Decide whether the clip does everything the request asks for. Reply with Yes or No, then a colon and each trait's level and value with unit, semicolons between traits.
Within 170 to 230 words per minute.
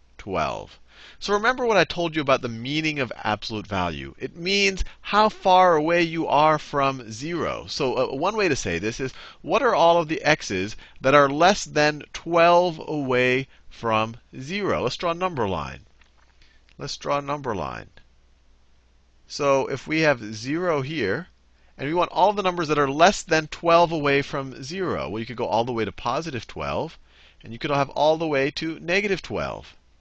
Yes: average, 190 wpm